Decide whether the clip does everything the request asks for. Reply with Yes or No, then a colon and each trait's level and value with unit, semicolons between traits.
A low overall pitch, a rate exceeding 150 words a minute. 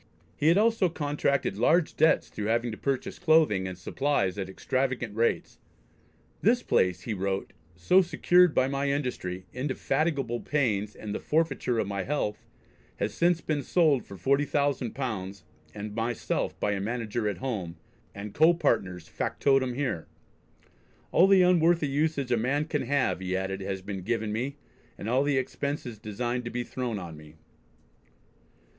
Yes: low, 125 Hz; average, 160 wpm